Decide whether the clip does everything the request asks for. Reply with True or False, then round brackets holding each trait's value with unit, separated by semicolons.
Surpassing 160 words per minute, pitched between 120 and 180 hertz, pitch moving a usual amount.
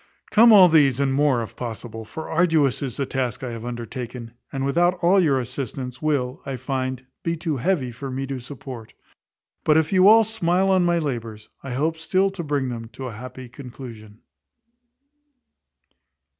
True (175 wpm; 135 Hz; 4.8 semitones)